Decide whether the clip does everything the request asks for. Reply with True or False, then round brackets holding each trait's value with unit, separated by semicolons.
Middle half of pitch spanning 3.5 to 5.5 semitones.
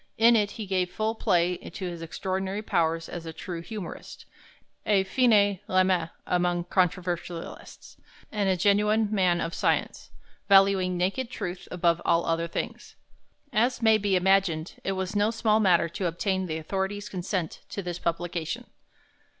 False (2.9 semitones)